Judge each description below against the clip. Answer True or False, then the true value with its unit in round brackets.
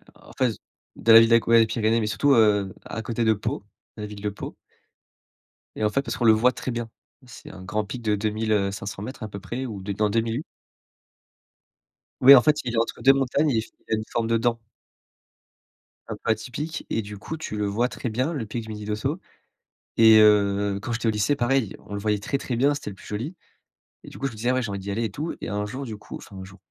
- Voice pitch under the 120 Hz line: True (110 Hz)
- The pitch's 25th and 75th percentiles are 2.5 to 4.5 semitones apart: True (2.9 semitones)